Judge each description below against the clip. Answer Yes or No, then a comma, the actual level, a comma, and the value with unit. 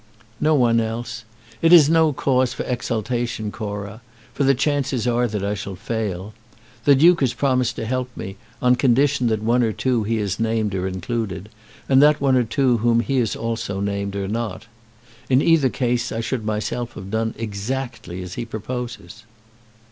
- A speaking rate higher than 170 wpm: Yes, average, 180 wpm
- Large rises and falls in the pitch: No, average, 3.3 semitones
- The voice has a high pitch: No, low, 115 Hz